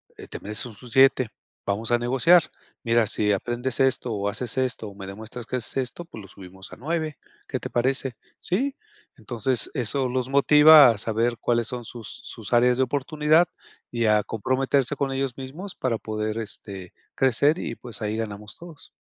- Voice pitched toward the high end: No, low, 120 Hz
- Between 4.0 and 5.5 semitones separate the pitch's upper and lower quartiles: No, average, 3.6 semitones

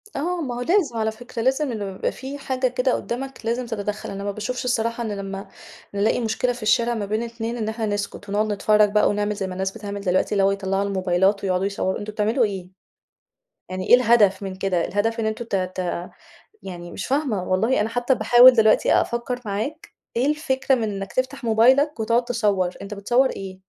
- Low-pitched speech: No, high, 220 Hz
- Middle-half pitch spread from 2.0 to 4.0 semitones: Yes, average, 3.6 semitones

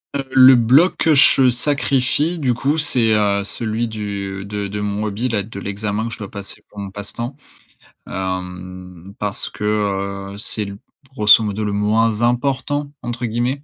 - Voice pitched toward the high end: No, low, 105 Hz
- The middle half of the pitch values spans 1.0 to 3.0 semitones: No, average, 3.7 semitones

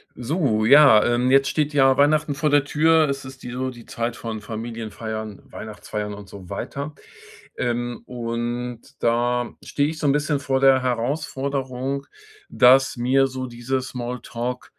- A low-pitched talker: Yes, low, 125 Hz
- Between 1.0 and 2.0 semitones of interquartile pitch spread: No, average, 2.7 semitones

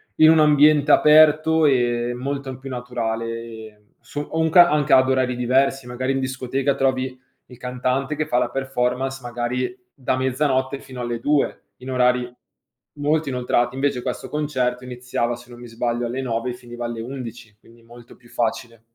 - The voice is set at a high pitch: No, low, 125 Hz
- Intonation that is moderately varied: No, narrow, 2.0 semitones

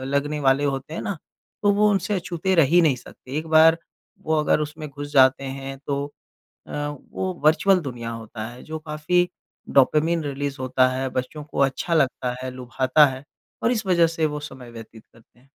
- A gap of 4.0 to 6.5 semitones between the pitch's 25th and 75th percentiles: No, average, 3.6 semitones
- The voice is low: No, medium, 145 Hz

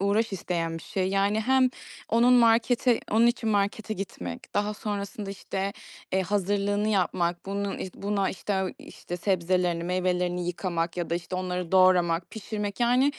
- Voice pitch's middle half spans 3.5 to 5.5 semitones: No, average, 2.8 semitones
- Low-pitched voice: No, high, 195 Hz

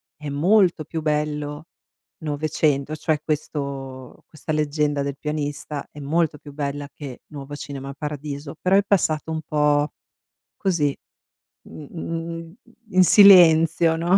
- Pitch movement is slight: Yes, narrow, 2.2 semitones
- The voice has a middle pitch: Yes, medium, 150 Hz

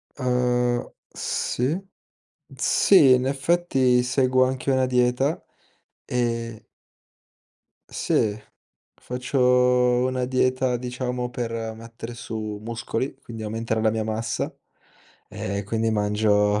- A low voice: Yes, low, 125 Hz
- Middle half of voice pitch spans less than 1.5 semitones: No, narrow, 2.4 semitones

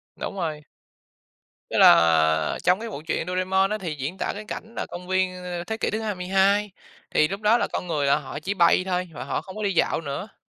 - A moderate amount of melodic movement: Yes, average, 4.1 semitones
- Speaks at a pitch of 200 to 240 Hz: No, medium, 185 Hz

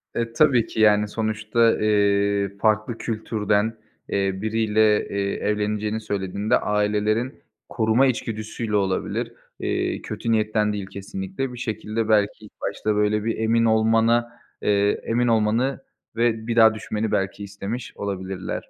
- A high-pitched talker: No, low, 110 Hz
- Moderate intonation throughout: No, narrow, 1.6 semitones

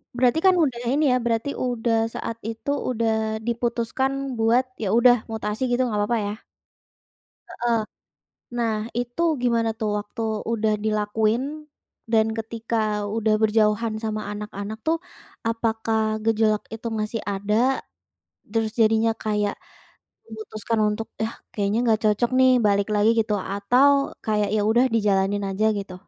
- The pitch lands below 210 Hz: No, high, 225 Hz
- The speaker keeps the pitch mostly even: Yes, narrow, 1.8 semitones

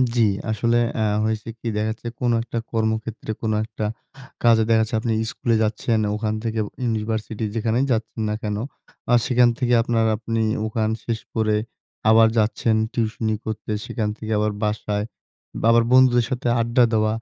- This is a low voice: Yes, low, 110 Hz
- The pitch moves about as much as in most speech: No, narrow, 1.3 semitones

